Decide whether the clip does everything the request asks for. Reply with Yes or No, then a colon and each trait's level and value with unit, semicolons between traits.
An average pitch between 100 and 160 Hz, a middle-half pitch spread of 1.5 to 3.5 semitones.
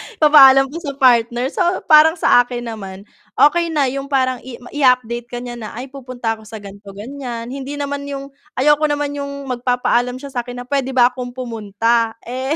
No: very high, 255 Hz; average, 2.8 semitones